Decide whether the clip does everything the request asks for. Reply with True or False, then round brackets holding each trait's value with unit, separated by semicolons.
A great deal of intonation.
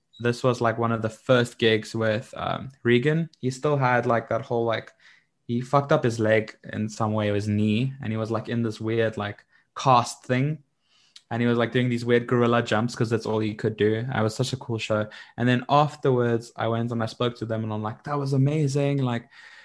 False (2.5 semitones)